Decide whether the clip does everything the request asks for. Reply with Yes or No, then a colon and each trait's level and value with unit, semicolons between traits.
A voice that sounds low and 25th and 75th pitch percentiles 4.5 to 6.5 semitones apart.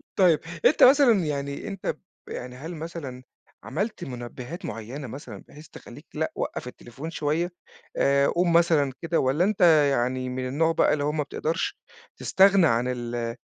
No: medium, 150 Hz; average, 5.0 semitones